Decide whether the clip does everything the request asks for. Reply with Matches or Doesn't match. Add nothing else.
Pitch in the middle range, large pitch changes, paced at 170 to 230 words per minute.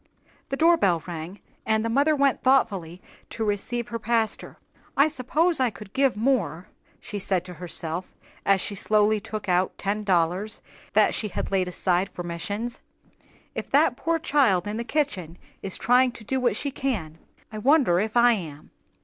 Doesn't match